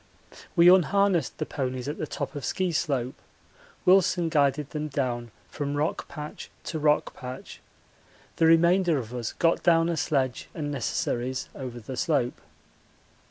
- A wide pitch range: No, average, 4.3 semitones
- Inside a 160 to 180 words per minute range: No, average, 150 wpm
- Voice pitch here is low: No, medium, 150 Hz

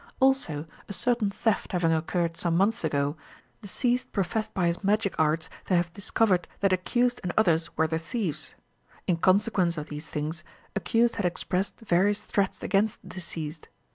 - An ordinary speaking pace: Yes, average, 160 wpm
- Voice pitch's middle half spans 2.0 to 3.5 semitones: No, average, 4.4 semitones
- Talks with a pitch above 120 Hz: Yes, medium, 185 Hz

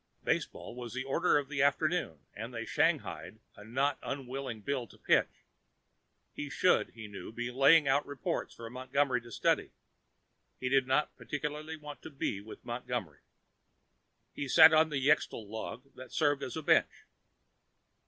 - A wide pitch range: No, average, 3.6 semitones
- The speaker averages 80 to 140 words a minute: No, average, 160 wpm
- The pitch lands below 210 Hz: Yes, low, 135 Hz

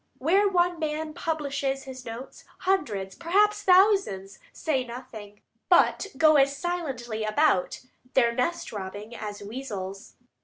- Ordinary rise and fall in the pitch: No, wide, 7.6 semitones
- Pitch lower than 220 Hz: No, very high, 270 Hz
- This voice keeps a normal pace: No, slow, 120 wpm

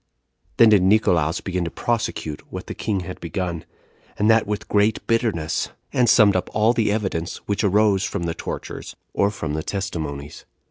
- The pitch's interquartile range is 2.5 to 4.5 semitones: Yes, average, 4.2 semitones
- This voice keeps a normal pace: Yes, average, 175 wpm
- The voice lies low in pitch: Yes, low, 100 Hz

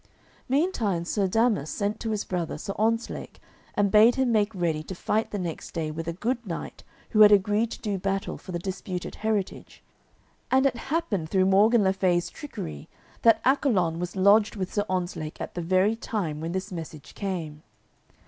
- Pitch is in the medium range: No, high, 195 Hz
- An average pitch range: Yes, average, 4.0 semitones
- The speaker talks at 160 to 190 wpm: Yes, average, 185 wpm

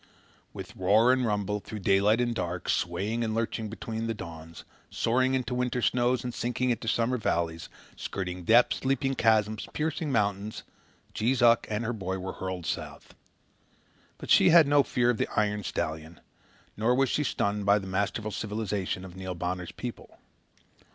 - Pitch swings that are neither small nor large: Yes, average, 4.2 semitones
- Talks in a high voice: No, low, 110 Hz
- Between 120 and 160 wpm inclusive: No, average, 170 wpm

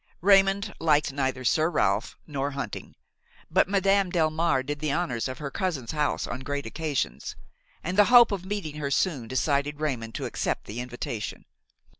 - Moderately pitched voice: Yes, medium, 150 Hz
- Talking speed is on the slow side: No, average, 165 wpm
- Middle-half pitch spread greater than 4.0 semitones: Yes, average, 5.3 semitones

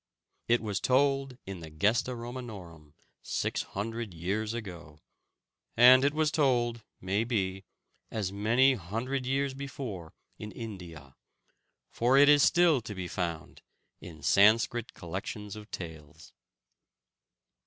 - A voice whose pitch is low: Yes, low, 110 Hz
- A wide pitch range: Yes, wide, 5.7 semitones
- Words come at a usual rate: No, slow, 120 wpm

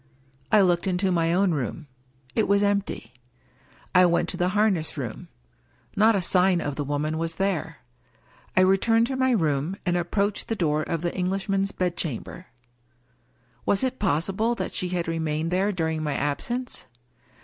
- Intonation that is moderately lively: Yes, average, 3.7 semitones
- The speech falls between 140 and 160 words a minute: No, average, 170 wpm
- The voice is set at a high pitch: No, medium, 180 Hz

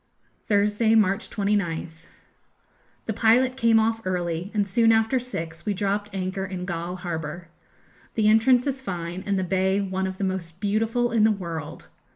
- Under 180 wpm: Yes, average, 165 wpm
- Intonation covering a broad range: No, average, 3.6 semitones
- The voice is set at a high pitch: Yes, high, 200 Hz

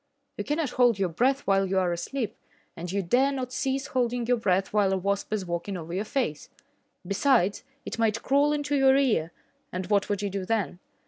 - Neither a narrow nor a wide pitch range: No, wide, 5.7 semitones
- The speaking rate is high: Yes, fast, 210 wpm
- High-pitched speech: Yes, high, 210 Hz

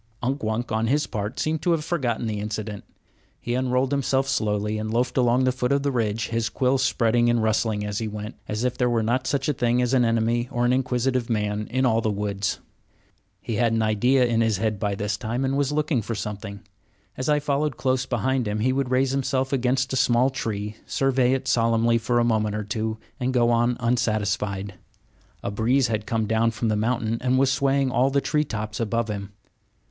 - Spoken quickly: Yes, fast, 215 wpm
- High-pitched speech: No, low, 120 Hz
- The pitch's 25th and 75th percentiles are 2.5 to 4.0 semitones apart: Yes, average, 3.2 semitones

